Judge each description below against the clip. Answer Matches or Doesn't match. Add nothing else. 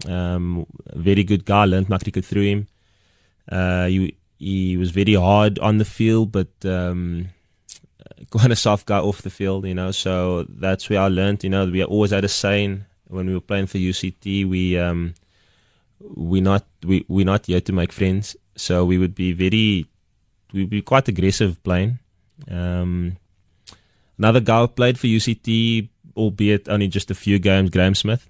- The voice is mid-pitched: Doesn't match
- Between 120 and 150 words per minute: Doesn't match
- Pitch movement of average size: Doesn't match